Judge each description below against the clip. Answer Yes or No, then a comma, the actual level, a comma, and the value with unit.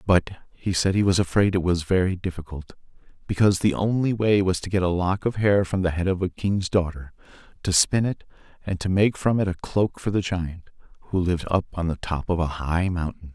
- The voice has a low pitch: Yes, very low, 90 Hz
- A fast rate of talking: Yes, fast, 230 wpm